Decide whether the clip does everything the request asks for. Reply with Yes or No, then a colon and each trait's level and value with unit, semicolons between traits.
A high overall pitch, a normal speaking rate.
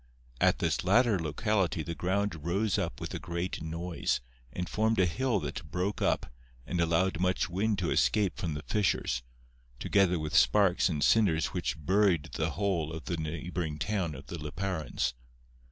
No: very low, 90 Hz; average, 170 wpm